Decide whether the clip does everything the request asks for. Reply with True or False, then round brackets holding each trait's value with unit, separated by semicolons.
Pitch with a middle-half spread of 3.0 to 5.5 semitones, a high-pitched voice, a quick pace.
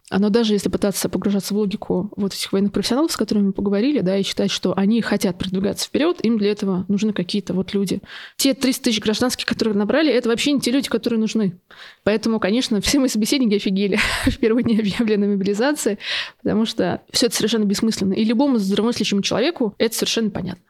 False (2.6 semitones; 215 Hz; 195 wpm)